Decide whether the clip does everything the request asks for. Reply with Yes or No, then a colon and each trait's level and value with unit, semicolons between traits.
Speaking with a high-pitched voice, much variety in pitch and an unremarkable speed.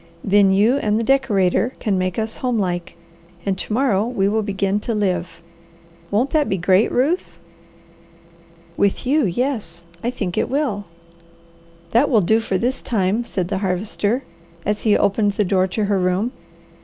No: high, 205 Hz; average, 3.9 semitones; average, 170 wpm